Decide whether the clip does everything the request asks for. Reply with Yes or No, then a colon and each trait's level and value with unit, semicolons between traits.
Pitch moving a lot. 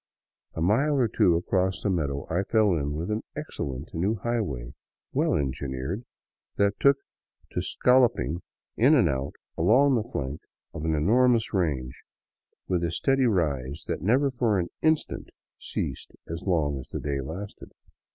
Yes: wide, 7.8 semitones